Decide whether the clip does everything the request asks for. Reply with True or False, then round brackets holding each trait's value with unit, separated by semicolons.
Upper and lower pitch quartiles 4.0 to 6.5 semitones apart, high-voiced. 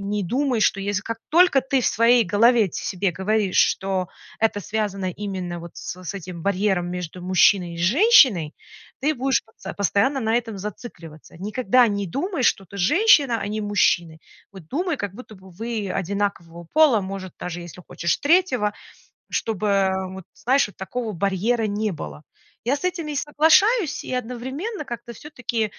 True (5.1 semitones; 210 Hz)